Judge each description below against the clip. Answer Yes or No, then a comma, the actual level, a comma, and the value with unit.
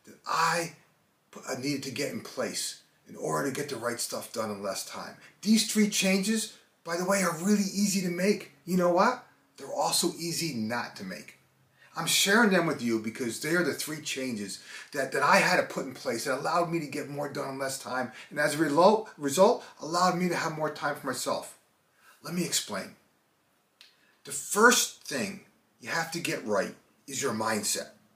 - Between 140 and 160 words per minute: No, average, 200 wpm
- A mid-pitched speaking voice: Yes, medium, 165 Hz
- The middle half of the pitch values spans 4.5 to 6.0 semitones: Yes, average, 5.3 semitones